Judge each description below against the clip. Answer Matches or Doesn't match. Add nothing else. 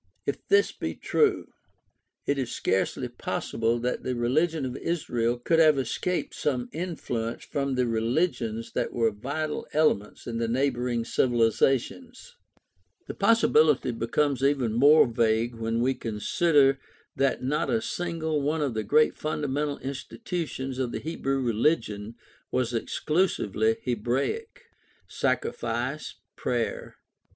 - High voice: Doesn't match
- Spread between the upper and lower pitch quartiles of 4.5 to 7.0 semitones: Matches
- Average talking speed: Doesn't match